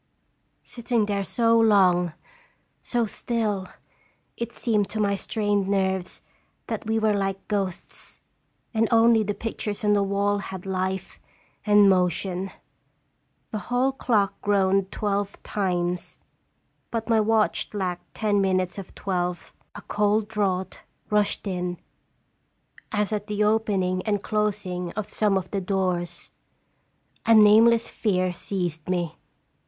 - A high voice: Yes, high, 200 Hz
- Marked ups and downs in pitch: No, narrow, 2.4 semitones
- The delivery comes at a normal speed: No, slow, 125 wpm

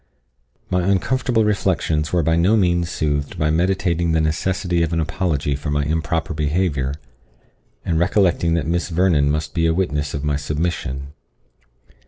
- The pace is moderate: Yes, average, 155 wpm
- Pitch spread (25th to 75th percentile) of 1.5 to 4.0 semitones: Yes, average, 3.2 semitones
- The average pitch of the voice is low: Yes, very low, 80 Hz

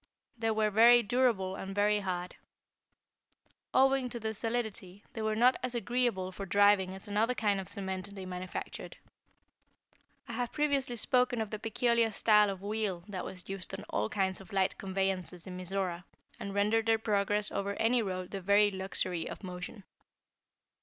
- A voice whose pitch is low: No, high, 205 Hz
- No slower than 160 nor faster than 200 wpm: Yes, average, 165 wpm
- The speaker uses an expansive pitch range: No, average, 3.0 semitones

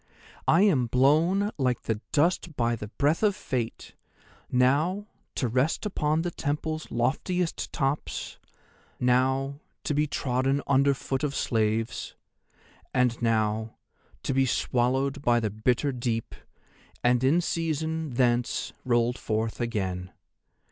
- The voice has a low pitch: Yes, low, 130 Hz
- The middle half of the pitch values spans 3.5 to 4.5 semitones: Yes, average, 4.1 semitones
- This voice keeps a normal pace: No, slow, 120 wpm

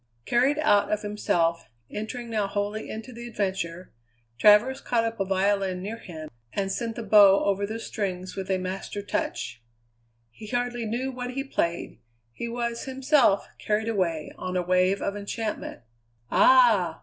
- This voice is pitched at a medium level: No, high, 210 Hz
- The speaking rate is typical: Yes, average, 160 wpm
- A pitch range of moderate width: Yes, average, 3.8 semitones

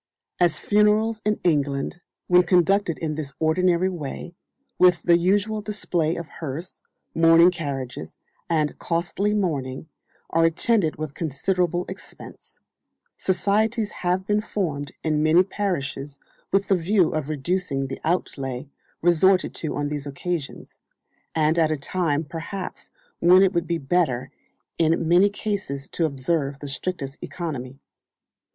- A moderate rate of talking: No, slow, 130 wpm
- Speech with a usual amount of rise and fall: Yes, average, 3.9 semitones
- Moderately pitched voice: Yes, medium, 170 Hz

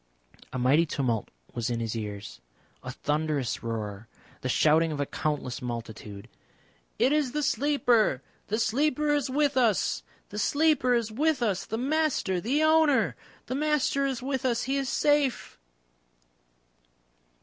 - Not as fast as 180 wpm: Yes, average, 145 wpm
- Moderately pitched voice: No, high, 230 Hz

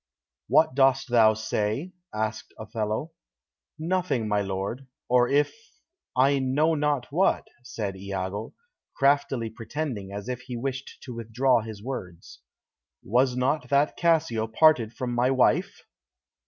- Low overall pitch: Yes, low, 125 Hz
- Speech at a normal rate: No, slow, 125 wpm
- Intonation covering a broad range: No, average, 4.3 semitones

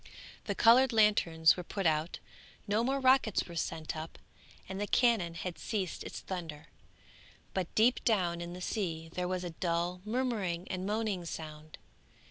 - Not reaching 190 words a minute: Yes, average, 160 wpm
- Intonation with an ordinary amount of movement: Yes, average, 4.4 semitones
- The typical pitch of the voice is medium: Yes, medium, 180 Hz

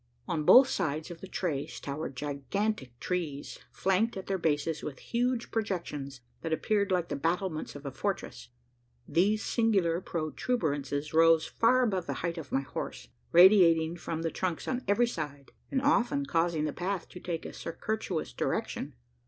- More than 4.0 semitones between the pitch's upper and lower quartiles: Yes, average, 4.9 semitones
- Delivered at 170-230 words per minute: No, average, 160 wpm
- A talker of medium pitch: Yes, medium, 170 Hz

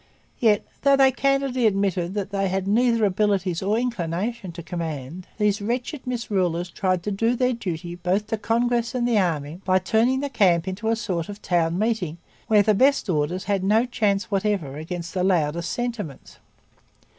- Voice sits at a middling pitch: No, high, 200 Hz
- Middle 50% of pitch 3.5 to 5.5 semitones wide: Yes, average, 4.6 semitones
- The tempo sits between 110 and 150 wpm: No, average, 180 wpm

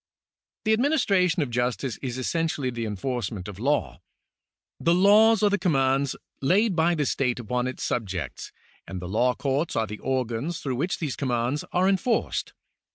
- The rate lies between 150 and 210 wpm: Yes, average, 165 wpm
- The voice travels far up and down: Yes, wide, 6.4 semitones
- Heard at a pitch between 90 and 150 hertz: Yes, low, 135 Hz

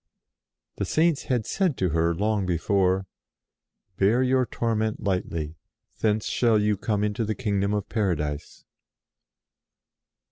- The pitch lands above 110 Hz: No, low, 105 Hz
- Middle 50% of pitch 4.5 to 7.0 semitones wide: No, average, 3.5 semitones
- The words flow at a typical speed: No, slow, 130 wpm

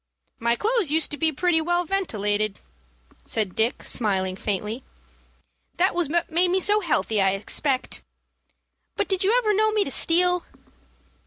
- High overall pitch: Yes, very high, 320 Hz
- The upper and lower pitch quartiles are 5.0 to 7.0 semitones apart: No, wide, 9.0 semitones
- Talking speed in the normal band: Yes, average, 155 wpm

